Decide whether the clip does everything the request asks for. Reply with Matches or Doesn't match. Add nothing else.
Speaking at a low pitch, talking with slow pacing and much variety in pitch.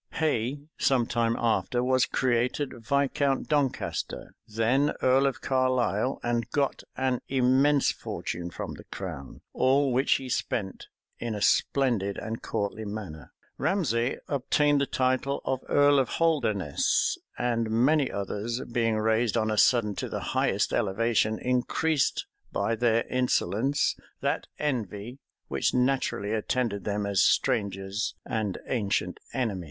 Doesn't match